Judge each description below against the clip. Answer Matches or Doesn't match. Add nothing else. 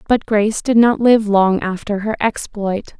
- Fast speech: Doesn't match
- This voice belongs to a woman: Matches